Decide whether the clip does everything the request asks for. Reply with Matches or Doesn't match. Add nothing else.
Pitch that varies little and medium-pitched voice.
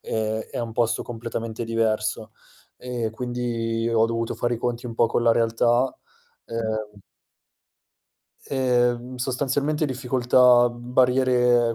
Doesn't match